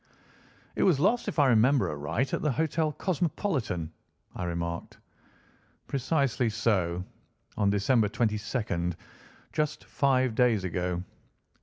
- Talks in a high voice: No, low, 115 Hz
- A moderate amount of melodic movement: No, wide, 7.5 semitones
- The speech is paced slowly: Yes, slow, 115 wpm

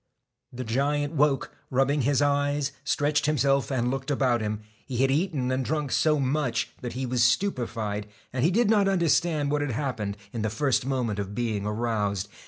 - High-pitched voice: No, low, 135 Hz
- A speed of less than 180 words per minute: No, average, 190 wpm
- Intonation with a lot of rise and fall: No, average, 3.7 semitones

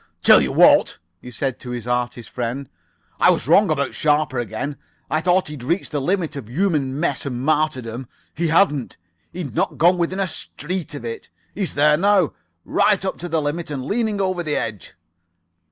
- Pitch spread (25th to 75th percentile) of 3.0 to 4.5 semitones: No, average, 5.3 semitones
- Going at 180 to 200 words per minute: Yes, average, 185 wpm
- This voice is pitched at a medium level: Yes, medium, 150 Hz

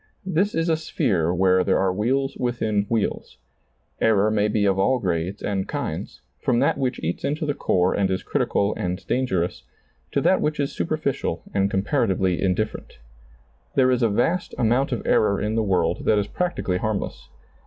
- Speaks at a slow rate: No, average, 175 wpm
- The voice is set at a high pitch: No, low, 105 Hz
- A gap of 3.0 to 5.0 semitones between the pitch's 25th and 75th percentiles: No, wide, 5.5 semitones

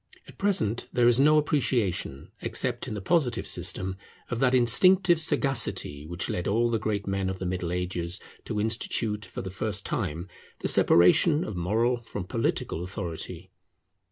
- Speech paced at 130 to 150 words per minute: No, average, 160 wpm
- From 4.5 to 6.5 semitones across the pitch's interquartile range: Yes, average, 5.2 semitones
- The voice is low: Yes, low, 105 Hz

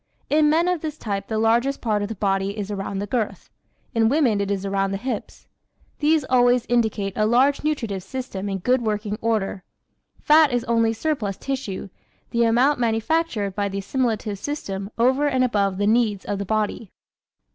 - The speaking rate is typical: Yes, average, 180 wpm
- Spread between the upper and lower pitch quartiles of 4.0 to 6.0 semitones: Yes, average, 4.5 semitones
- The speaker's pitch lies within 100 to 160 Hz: No, high, 225 Hz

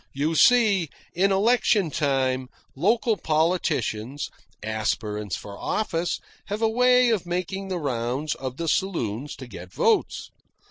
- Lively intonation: Yes, wide, 7.4 semitones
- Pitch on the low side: No, medium, 160 Hz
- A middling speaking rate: No, slow, 130 wpm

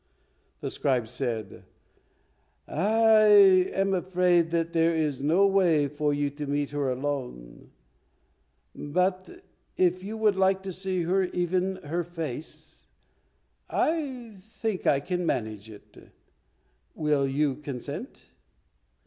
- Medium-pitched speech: Yes, medium, 165 Hz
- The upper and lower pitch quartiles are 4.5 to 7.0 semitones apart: Yes, average, 4.9 semitones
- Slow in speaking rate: Yes, slow, 115 wpm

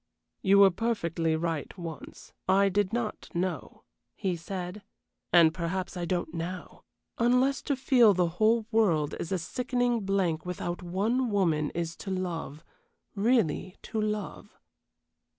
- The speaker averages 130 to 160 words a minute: Yes, slow, 135 wpm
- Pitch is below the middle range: No, medium, 185 Hz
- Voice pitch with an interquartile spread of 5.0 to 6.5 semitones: No, average, 4.2 semitones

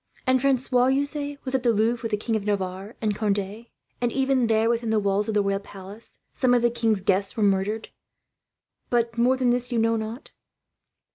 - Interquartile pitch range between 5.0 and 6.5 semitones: No, average, 3.1 semitones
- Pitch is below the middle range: No, high, 225 Hz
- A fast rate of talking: Yes, fast, 210 wpm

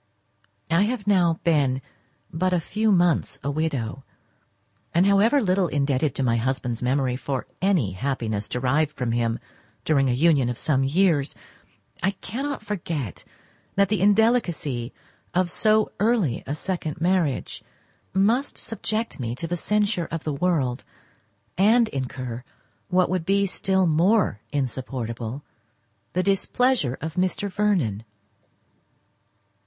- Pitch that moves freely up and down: Yes, wide, 6.9 semitones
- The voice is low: No, medium, 165 Hz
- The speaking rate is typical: No, slow, 130 wpm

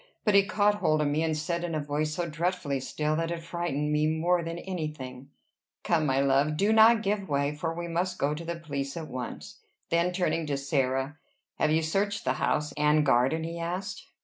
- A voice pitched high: No, medium, 160 Hz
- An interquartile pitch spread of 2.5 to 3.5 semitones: Yes, average, 3.0 semitones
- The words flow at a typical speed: No, fast, 215 wpm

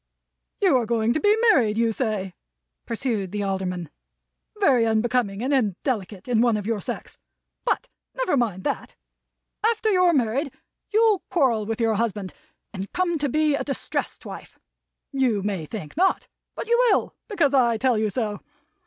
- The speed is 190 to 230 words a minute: No, average, 160 wpm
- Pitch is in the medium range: No, high, 235 Hz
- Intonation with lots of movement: Yes, wide, 5.7 semitones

